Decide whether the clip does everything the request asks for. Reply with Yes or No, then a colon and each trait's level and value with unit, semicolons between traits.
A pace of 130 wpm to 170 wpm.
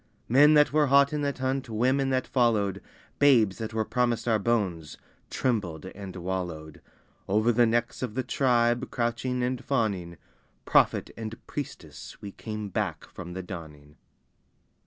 Yes: average, 150 wpm